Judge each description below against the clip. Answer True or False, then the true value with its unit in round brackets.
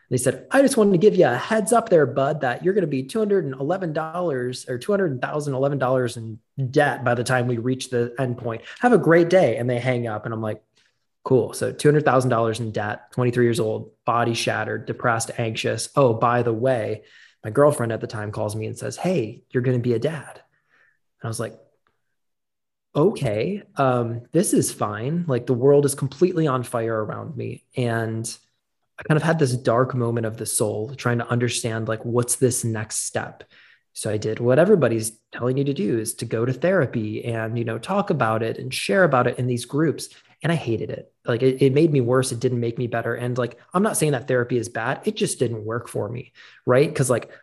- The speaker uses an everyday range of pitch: True (3.6 semitones)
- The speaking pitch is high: False (125 Hz)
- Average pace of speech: False (215 wpm)